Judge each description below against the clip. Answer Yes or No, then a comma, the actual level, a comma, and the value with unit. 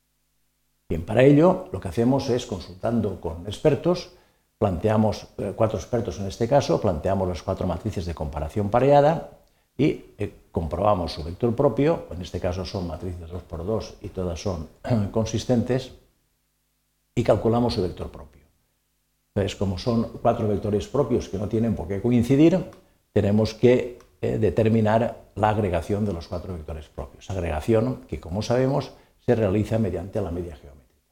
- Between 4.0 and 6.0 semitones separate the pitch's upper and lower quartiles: Yes, average, 4.6 semitones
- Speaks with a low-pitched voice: Yes, low, 105 Hz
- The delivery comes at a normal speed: Yes, average, 150 wpm